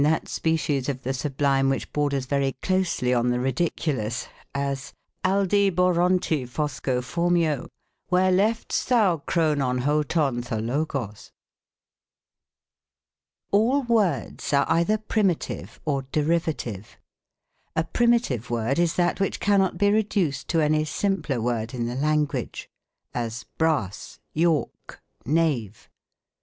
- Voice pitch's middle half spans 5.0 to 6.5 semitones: Yes, wide, 5.5 semitones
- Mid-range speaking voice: Yes, medium, 150 Hz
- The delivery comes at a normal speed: No, slow, 105 wpm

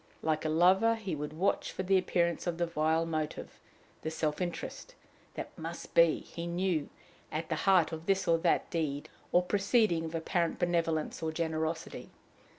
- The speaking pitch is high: No, medium, 170 Hz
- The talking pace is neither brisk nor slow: Yes, average, 170 wpm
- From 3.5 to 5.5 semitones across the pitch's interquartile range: No, narrow, 2.5 semitones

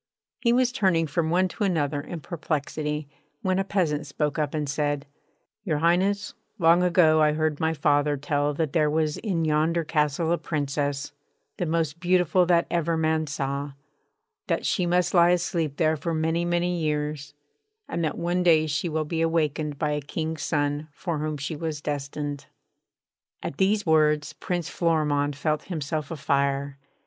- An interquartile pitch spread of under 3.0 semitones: Yes, narrow, 2.6 semitones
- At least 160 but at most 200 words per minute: Yes, average, 170 wpm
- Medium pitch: Yes, medium, 155 Hz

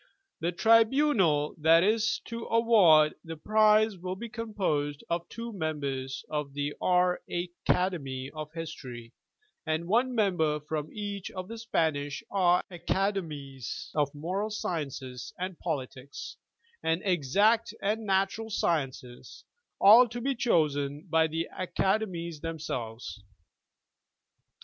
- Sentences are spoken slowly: Yes, slow, 120 wpm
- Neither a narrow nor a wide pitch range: No, wide, 6.0 semitones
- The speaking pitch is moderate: Yes, medium, 175 Hz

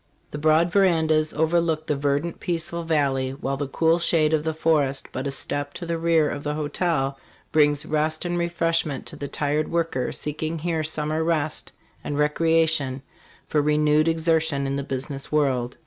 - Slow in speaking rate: No, average, 175 wpm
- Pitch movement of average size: No, narrow, 2.3 semitones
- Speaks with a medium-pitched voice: Yes, medium, 155 Hz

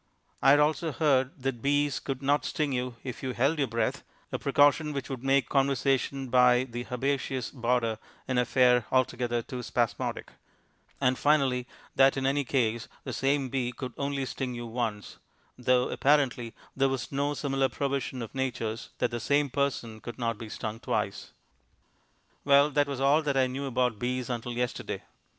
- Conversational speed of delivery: Yes, average, 175 wpm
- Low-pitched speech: Yes, low, 130 Hz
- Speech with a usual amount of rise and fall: No, narrow, 2.2 semitones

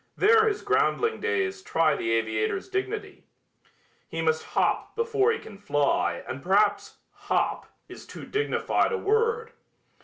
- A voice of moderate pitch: No, very high, 385 Hz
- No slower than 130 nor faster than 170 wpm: Yes, average, 140 wpm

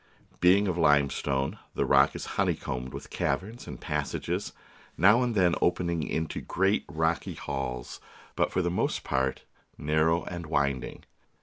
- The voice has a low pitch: Yes, very low, 80 Hz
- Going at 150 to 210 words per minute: No, average, 140 wpm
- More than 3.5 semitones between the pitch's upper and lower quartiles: Yes, average, 4.6 semitones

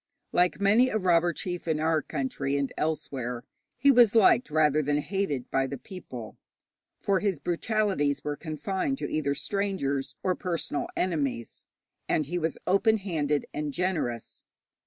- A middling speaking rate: Yes, average, 150 wpm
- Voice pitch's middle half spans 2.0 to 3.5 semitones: No, average, 5.2 semitones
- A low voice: No, medium, 160 Hz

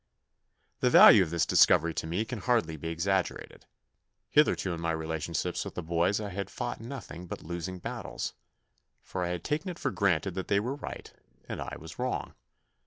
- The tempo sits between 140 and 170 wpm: No, average, 185 wpm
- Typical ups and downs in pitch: Yes, average, 4.3 semitones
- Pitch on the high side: No, very low, 90 Hz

